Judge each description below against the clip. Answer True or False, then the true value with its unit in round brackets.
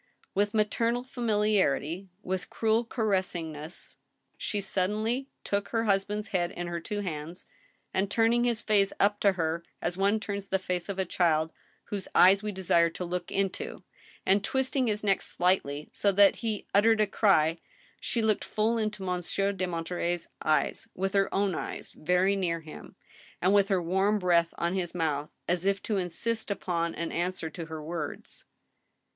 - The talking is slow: False (170 wpm)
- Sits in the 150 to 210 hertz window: True (190 Hz)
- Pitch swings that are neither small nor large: True (3.3 semitones)